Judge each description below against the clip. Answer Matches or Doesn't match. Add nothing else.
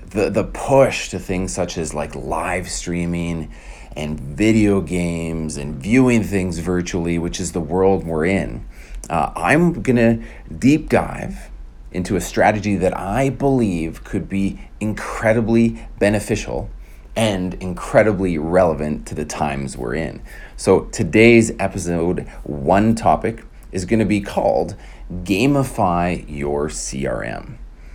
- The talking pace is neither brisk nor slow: Doesn't match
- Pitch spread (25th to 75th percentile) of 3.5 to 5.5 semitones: Matches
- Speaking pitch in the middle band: Doesn't match